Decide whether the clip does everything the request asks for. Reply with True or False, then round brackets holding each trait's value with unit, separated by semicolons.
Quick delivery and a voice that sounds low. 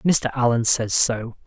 False (165 wpm; 120 Hz)